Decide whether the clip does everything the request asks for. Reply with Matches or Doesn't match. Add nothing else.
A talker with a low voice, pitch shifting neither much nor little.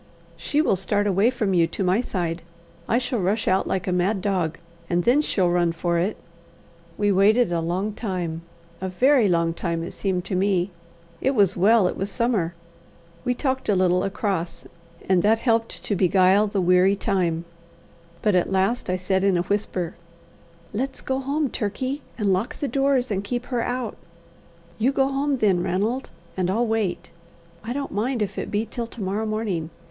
Doesn't match